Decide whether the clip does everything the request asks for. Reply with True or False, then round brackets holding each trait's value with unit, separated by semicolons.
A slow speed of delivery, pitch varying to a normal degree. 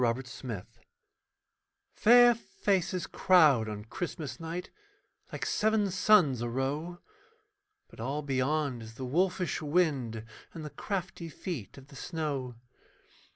False (120 wpm; 6.0 semitones)